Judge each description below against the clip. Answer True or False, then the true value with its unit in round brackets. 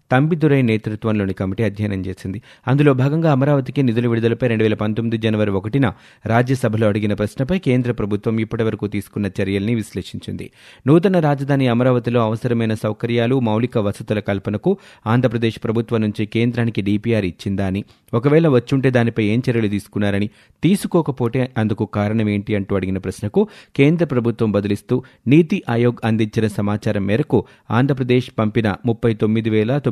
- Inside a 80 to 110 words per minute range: False (125 wpm)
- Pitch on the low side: True (115 Hz)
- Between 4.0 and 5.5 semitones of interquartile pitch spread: False (3.3 semitones)